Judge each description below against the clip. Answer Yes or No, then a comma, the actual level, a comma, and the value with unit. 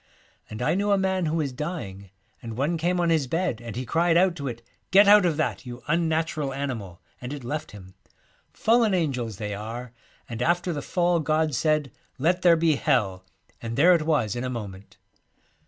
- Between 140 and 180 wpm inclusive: No, fast, 205 wpm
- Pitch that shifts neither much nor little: No, wide, 6.2 semitones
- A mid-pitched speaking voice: Yes, medium, 150 Hz